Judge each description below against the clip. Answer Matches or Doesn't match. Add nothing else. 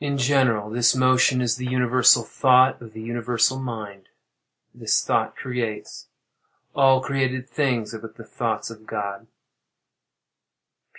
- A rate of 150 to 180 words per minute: Doesn't match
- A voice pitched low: Matches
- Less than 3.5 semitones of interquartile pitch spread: Matches